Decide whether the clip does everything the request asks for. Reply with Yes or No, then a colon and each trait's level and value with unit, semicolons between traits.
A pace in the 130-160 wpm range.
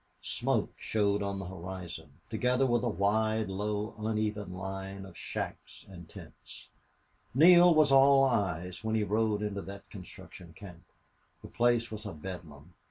Yes: average, 150 wpm